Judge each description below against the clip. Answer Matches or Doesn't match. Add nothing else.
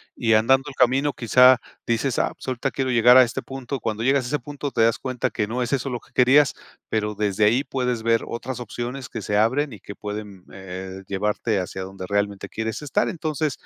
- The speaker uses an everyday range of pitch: Matches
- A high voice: Doesn't match